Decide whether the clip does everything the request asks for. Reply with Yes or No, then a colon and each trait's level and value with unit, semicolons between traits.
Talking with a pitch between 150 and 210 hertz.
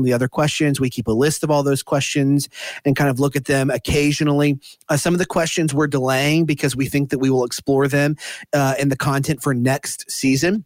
No: medium, 140 Hz